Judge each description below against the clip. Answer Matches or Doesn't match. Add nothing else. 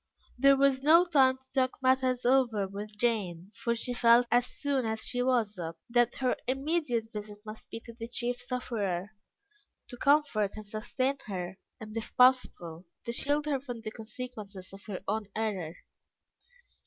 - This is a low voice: Doesn't match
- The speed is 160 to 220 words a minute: Matches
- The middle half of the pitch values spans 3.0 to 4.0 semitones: Matches